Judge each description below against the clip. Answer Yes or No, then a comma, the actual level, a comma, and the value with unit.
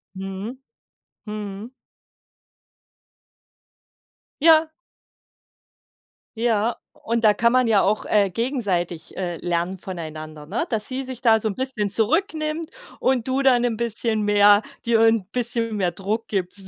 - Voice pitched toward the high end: Yes, high, 220 Hz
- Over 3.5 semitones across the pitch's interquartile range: Yes, average, 3.9 semitones